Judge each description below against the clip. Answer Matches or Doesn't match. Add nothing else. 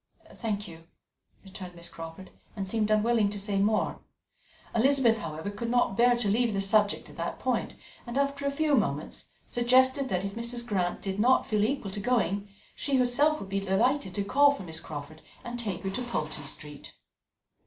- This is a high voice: Matches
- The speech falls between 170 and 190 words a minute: Matches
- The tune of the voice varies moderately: Matches